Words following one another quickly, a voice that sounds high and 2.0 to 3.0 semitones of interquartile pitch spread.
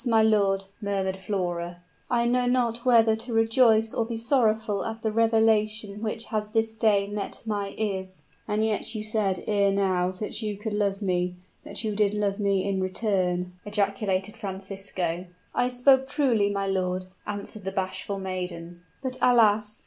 No: average, 165 wpm; high, 210 Hz; narrow, 2.5 semitones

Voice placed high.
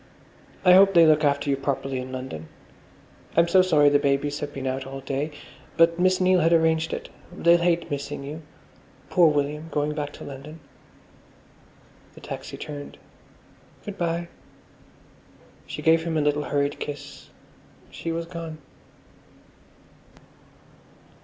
No: medium, 150 Hz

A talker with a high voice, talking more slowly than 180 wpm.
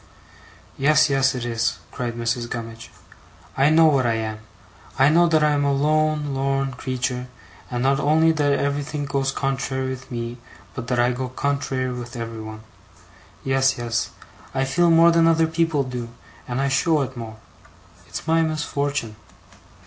No: low, 135 Hz; average, 165 wpm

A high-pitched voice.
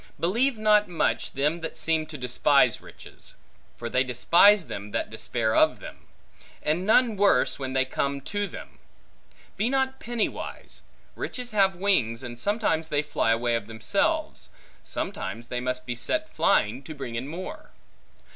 No: medium, 155 Hz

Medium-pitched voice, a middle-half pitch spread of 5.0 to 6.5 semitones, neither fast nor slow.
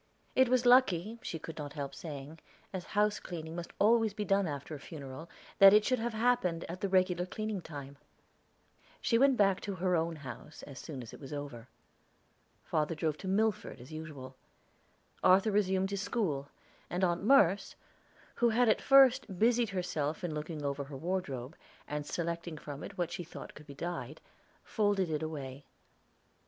Yes: medium, 175 Hz; wide, 5.5 semitones; average, 175 wpm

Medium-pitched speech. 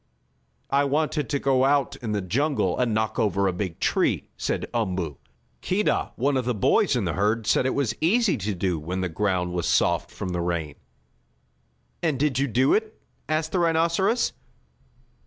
No: low, 120 Hz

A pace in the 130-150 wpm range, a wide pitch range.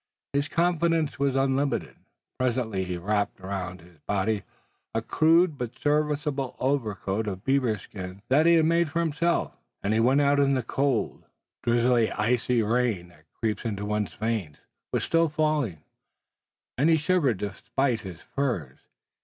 Yes: average, 145 wpm; wide, 6.0 semitones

